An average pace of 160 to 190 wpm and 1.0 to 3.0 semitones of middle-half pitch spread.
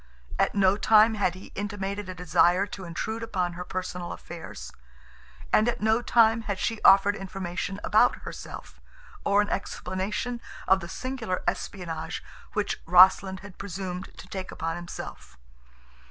No: average, 145 wpm; average, 2.7 semitones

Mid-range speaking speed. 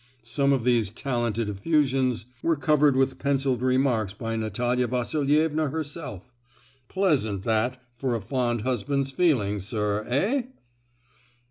No: slow, 120 wpm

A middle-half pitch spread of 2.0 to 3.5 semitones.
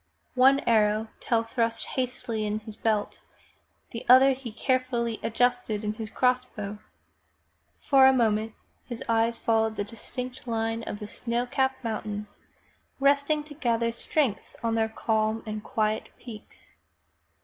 Yes: narrow, 2.6 semitones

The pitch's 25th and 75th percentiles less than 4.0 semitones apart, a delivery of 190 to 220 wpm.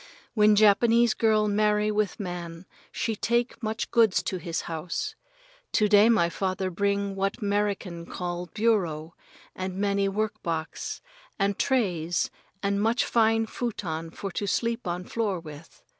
No: average, 3.5 semitones; average, 145 wpm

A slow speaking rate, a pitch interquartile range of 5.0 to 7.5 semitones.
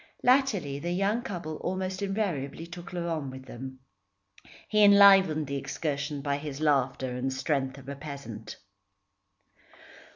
Yes: slow, 130 wpm; wide, 5.4 semitones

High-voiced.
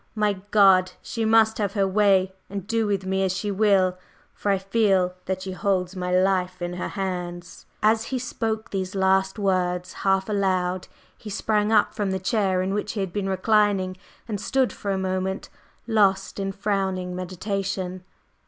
Yes: high, 195 Hz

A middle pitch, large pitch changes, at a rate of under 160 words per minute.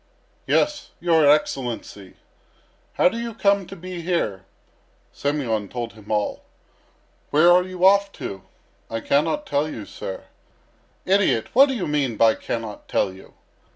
Yes: medium, 150 Hz; wide, 8.7 semitones; average, 145 wpm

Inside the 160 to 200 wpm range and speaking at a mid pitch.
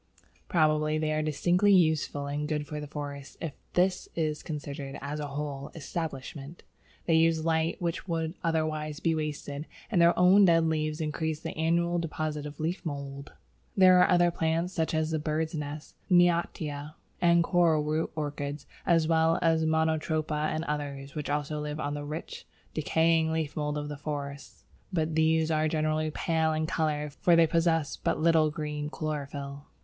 Yes: average, 165 wpm; medium, 155 Hz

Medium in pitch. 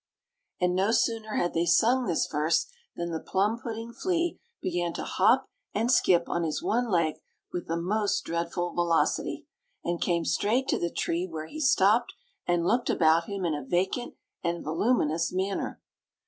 Yes: medium, 175 Hz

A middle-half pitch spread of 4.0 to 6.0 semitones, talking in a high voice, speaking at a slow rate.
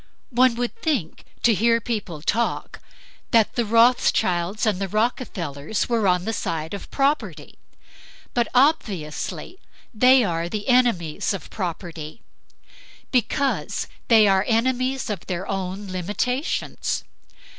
Yes: average, 5.2 semitones; high, 215 Hz; slow, 120 wpm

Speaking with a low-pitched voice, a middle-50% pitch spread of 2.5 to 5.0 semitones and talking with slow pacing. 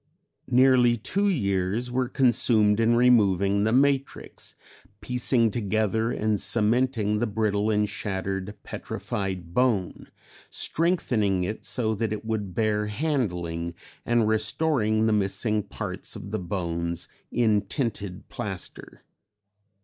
Yes: low, 110 Hz; average, 3.5 semitones; slow, 115 wpm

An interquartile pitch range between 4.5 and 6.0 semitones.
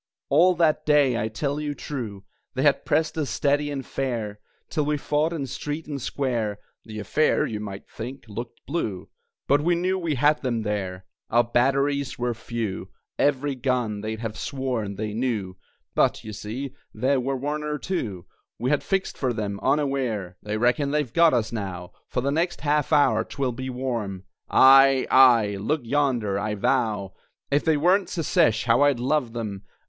Yes: average, 5.0 semitones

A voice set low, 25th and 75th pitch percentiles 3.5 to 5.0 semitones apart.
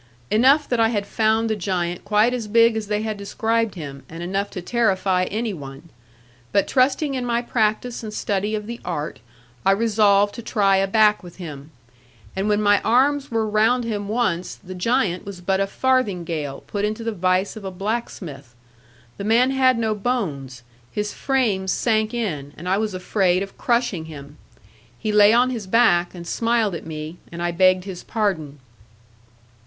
No: high, 205 Hz; average, 4.0 semitones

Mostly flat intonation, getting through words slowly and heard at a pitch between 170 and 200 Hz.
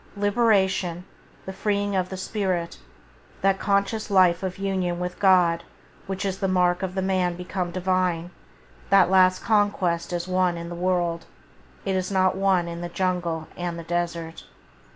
No: narrow, 1.8 semitones; average, 160 wpm; medium, 185 Hz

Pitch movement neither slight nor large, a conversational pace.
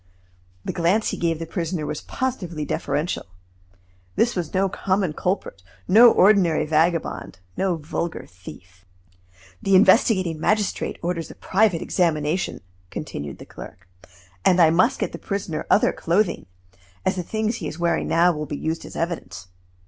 Yes: average, 3.7 semitones; average, 150 wpm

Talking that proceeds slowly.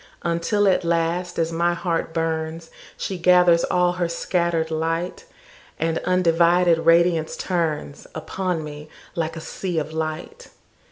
Yes: slow, 115 wpm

